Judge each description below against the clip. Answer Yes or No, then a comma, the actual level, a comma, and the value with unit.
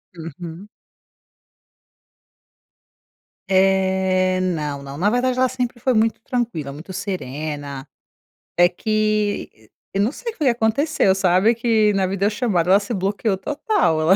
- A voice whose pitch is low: No, high, 195 Hz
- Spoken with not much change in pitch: No, average, 4.5 semitones